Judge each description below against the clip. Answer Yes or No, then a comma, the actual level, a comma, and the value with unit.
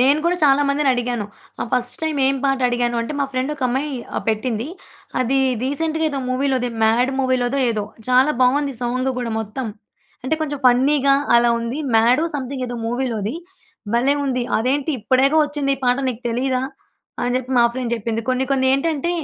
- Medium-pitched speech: No, very high, 255 Hz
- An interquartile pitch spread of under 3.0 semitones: Yes, narrow, 2.4 semitones